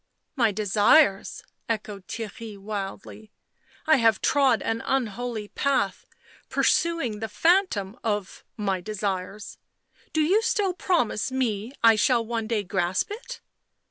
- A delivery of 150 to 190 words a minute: No, average, 140 wpm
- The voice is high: Yes, high, 225 Hz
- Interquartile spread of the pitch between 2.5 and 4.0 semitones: No, average, 4.6 semitones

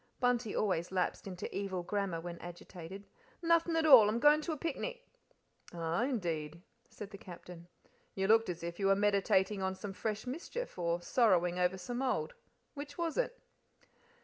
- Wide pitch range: Yes, wide, 6.2 semitones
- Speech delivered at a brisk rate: No, average, 170 wpm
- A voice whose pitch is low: No, high, 200 Hz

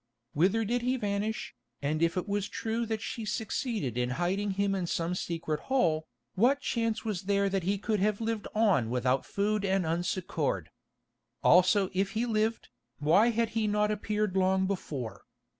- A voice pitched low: No, high, 200 Hz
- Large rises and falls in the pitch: No, average, 4.0 semitones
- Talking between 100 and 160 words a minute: No, average, 170 wpm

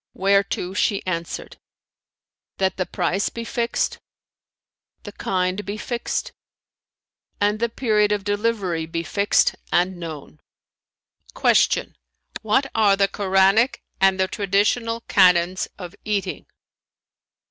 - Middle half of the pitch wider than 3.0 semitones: No, narrow, 2.4 semitones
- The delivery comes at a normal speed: No, slow, 110 wpm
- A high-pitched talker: Yes, high, 195 Hz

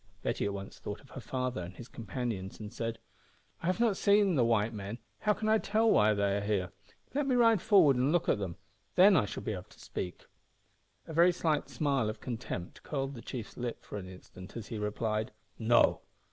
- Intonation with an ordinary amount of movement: No, wide, 8.5 semitones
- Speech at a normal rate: No, fast, 215 wpm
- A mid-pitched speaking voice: No, low, 120 Hz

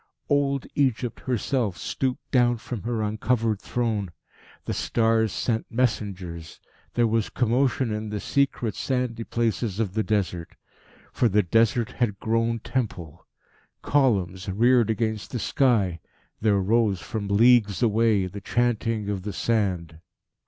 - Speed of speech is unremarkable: No, slow, 130 wpm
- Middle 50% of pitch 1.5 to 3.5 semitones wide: Yes, average, 3.1 semitones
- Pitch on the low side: Yes, low, 110 Hz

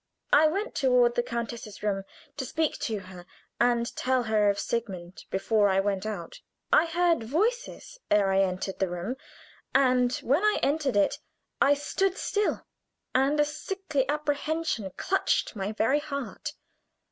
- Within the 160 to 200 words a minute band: No, average, 150 wpm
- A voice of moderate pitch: No, very high, 250 Hz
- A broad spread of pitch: Yes, wide, 6.7 semitones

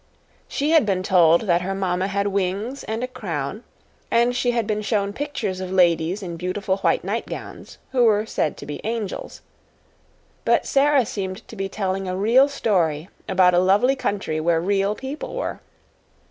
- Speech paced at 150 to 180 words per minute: Yes, average, 175 wpm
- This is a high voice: Yes, high, 200 Hz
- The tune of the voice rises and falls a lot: No, average, 4.1 semitones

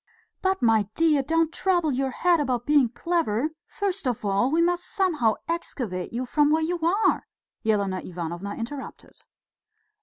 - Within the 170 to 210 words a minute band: No, average, 150 wpm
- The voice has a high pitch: Yes, very high, 290 Hz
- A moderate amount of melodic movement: No, wide, 7.2 semitones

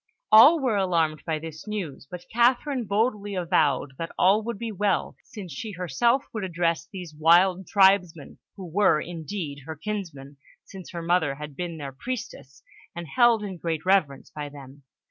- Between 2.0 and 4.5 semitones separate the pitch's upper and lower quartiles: No, average, 4.9 semitones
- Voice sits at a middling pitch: Yes, medium, 180 Hz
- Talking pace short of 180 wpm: Yes, average, 165 wpm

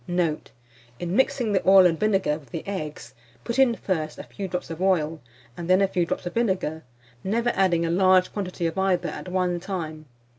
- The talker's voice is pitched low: No, medium, 180 Hz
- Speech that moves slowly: No, average, 200 wpm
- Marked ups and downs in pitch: No, average, 2.7 semitones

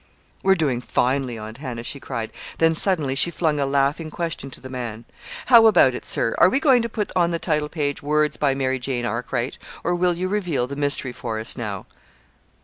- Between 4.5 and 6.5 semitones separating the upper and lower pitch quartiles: Yes, average, 5.3 semitones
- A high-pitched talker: No, medium, 140 Hz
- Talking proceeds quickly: Yes, fast, 210 wpm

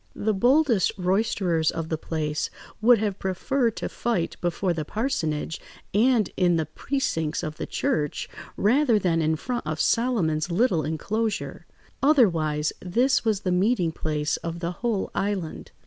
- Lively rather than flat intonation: Yes, wide, 6.1 semitones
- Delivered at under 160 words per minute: Yes, average, 150 wpm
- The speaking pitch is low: No, medium, 185 Hz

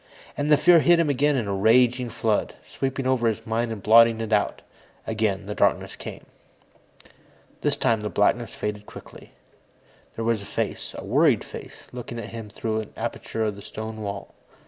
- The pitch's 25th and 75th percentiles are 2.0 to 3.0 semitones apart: Yes, average, 2.7 semitones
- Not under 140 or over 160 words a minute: No, average, 185 wpm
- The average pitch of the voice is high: No, low, 115 Hz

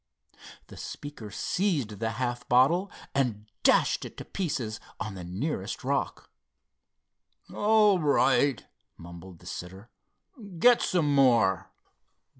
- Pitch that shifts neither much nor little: No, wide, 7.3 semitones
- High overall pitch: No, low, 125 Hz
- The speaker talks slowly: Yes, slow, 115 wpm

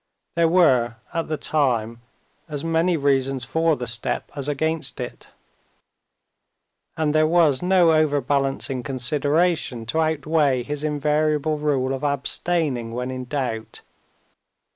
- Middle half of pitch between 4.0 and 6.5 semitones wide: No, average, 3.4 semitones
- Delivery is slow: Yes, slow, 120 wpm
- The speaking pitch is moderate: Yes, medium, 145 Hz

